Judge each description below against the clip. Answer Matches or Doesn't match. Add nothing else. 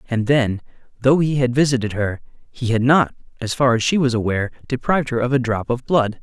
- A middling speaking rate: Doesn't match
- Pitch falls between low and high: Doesn't match